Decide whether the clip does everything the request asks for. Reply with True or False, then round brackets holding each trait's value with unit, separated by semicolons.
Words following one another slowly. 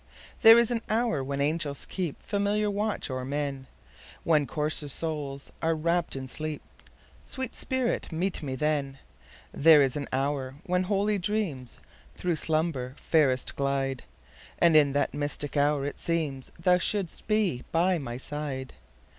True (125 wpm)